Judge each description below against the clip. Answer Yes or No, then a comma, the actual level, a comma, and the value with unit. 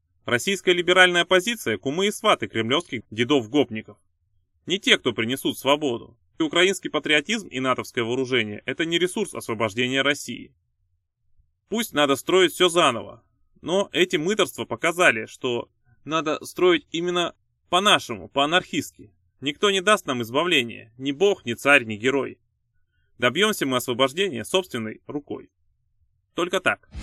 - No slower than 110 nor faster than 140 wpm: Yes, average, 125 wpm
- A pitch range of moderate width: No, wide, 7.8 semitones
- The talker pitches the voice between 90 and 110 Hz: No, medium, 140 Hz